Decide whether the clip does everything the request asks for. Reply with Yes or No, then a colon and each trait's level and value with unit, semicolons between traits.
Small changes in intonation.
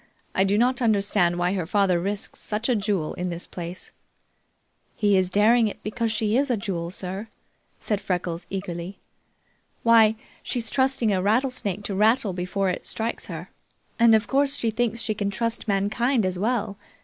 No: average, 3.5 semitones